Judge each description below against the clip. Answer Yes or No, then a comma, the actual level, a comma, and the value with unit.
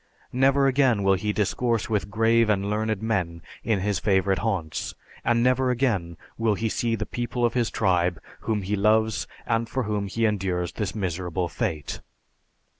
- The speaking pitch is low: Yes, low, 105 Hz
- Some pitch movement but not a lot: Yes, average, 3.3 semitones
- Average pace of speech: Yes, average, 170 wpm